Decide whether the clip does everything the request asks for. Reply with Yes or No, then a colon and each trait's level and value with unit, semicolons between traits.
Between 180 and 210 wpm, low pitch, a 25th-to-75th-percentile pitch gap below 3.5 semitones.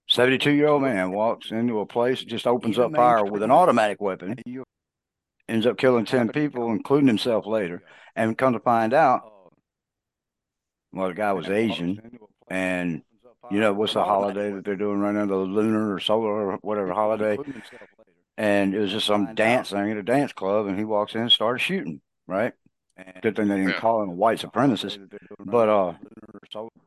Yes: average, 185 wpm; low, 105 Hz; average, 2.8 semitones